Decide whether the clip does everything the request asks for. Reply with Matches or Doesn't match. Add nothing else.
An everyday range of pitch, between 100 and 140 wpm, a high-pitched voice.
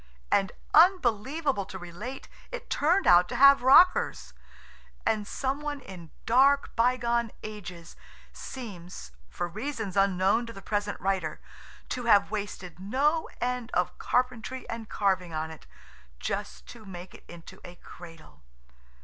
Doesn't match